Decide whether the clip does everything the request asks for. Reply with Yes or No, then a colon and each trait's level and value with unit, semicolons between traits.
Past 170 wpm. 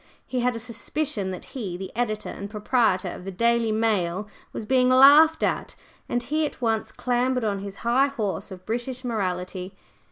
Yes: average, 180 wpm